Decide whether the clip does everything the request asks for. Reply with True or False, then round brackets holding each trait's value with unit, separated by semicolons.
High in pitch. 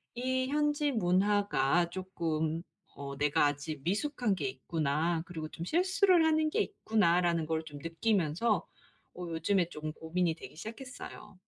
False (175 Hz)